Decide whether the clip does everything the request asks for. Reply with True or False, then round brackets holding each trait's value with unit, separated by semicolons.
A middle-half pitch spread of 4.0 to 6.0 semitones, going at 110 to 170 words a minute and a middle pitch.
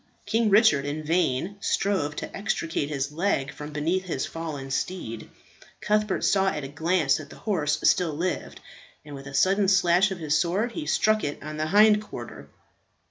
False (5.0 semitones; 180 wpm; 165 Hz)